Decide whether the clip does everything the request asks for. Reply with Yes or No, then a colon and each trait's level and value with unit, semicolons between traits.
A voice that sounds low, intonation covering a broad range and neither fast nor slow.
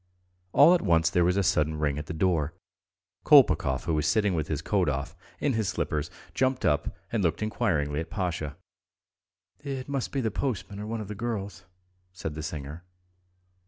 Yes: very low, 90 Hz; wide, 5.8 semitones; average, 185 wpm